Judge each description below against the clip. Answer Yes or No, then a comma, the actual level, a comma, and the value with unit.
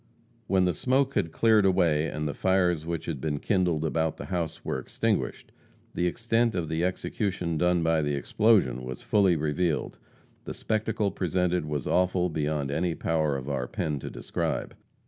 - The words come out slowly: No, average, 170 wpm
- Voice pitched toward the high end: No, very low, 85 Hz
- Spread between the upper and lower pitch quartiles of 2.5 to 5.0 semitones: Yes, average, 3.7 semitones